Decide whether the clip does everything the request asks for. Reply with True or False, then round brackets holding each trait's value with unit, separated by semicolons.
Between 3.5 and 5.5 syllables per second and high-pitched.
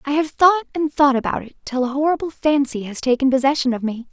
False (6.2 syllables/s; 275 Hz)